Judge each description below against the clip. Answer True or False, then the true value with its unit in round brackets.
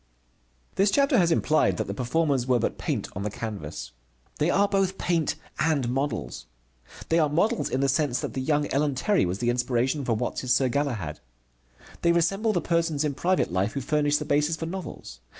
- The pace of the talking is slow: False (195 wpm)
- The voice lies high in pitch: False (145 Hz)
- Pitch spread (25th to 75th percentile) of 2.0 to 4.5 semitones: False (5.5 semitones)